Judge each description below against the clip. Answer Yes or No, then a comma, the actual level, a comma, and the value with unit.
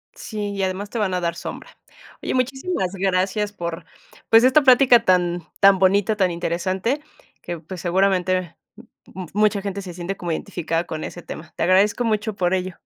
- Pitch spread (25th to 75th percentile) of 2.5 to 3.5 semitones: Yes, average, 3.0 semitones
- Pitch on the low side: No, high, 190 Hz